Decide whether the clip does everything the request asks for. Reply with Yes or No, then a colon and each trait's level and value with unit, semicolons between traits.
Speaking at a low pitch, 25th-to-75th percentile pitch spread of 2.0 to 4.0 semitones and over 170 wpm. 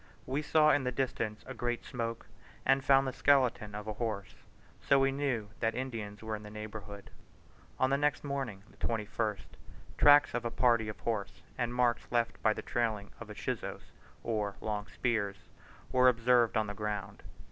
Yes: low, 115 Hz; average, 3.3 semitones; average, 180 wpm